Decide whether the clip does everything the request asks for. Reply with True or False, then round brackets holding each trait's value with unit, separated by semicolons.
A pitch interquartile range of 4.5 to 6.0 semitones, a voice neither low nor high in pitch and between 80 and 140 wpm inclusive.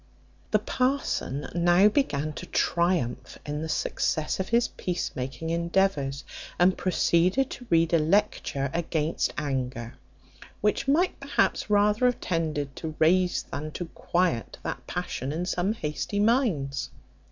True (4.8 semitones; 170 Hz; 135 wpm)